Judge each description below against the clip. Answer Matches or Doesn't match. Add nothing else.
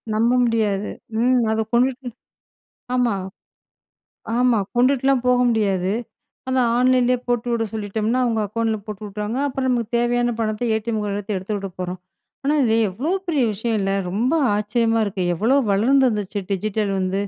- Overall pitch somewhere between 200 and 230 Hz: Matches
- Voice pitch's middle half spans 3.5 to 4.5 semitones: Doesn't match